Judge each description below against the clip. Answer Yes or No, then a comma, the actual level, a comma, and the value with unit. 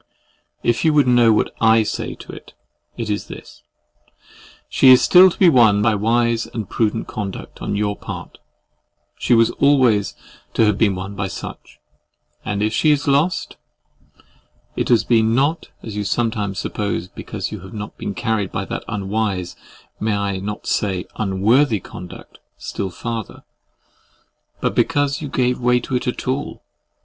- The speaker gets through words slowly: No, average, 155 wpm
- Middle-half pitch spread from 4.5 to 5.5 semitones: No, average, 3.5 semitones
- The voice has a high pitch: No, low, 110 Hz